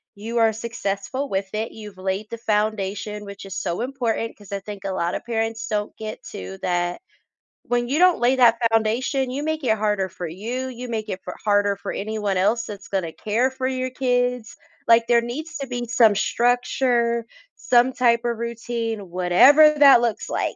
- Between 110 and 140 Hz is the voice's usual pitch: No, high, 225 Hz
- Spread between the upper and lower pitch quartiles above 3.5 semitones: No, average, 3.2 semitones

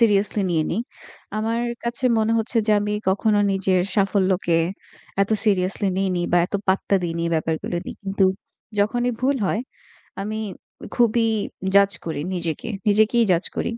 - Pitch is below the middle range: No, high, 200 Hz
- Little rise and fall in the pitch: No, average, 3.1 semitones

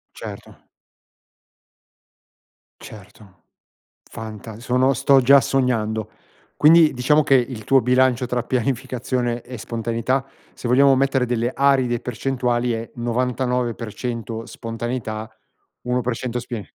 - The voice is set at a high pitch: No, low, 125 Hz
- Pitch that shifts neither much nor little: No, narrow, 2.1 semitones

